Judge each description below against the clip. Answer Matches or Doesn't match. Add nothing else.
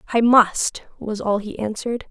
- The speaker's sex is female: Matches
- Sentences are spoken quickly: Doesn't match